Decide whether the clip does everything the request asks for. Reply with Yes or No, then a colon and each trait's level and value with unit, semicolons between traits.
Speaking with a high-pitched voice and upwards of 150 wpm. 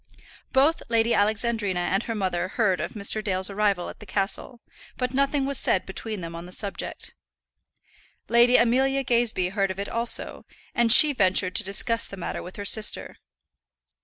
Yes: high, 210 Hz; average, 170 wpm